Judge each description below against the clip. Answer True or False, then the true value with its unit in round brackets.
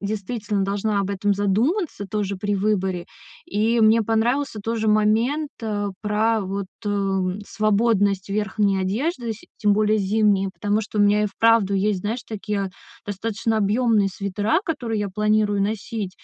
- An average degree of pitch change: False (1.8 semitones)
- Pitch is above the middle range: True (210 Hz)